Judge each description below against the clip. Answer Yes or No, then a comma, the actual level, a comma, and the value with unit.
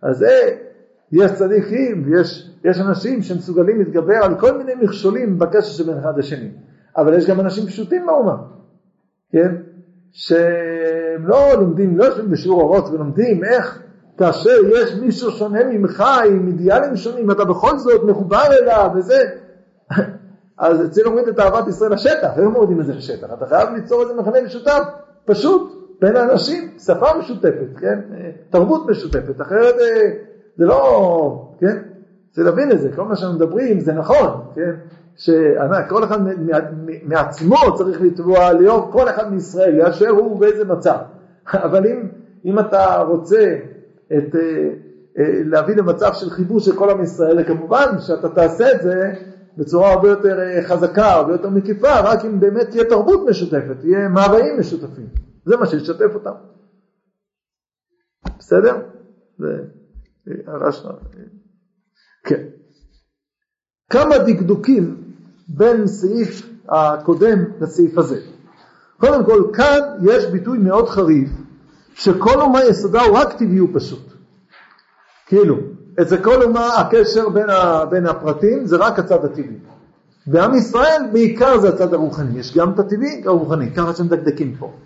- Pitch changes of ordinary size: Yes, average, 4.8 semitones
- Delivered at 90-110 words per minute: No, average, 135 wpm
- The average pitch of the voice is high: Yes, high, 195 Hz